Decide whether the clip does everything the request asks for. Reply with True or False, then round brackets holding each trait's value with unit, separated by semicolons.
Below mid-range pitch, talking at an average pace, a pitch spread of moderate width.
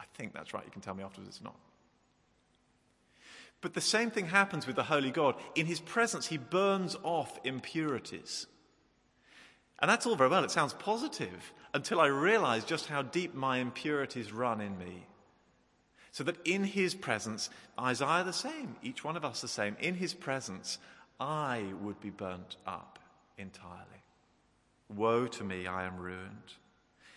False (125 Hz; 165 wpm; 9.0 semitones)